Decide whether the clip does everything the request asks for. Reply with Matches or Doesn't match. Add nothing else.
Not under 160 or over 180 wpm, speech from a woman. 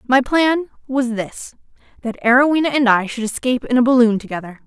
Matches